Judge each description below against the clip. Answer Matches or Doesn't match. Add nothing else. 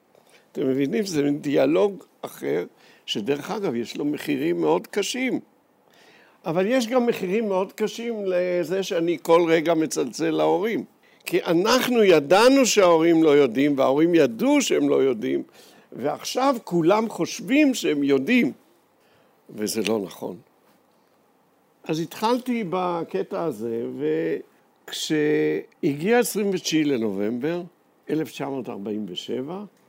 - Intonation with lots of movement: Matches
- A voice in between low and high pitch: Matches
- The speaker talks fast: Doesn't match